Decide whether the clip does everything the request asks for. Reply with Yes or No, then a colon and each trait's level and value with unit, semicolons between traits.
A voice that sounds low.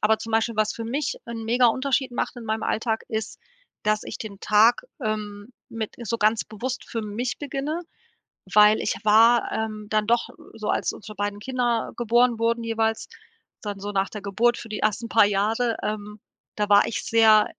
No: high, 220 Hz